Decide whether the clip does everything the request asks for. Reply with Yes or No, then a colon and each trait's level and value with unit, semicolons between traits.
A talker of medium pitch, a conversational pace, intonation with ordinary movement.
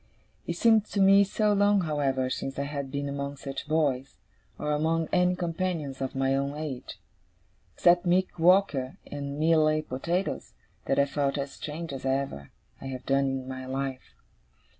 Yes: medium, 145 Hz; average, 165 wpm; average, 4.1 semitones